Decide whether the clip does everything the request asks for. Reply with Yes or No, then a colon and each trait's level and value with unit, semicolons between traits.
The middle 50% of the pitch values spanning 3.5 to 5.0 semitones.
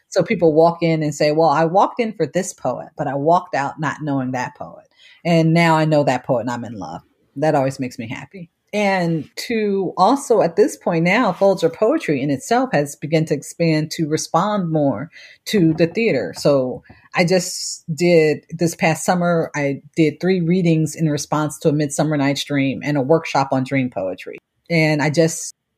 No: average, 3.0 semitones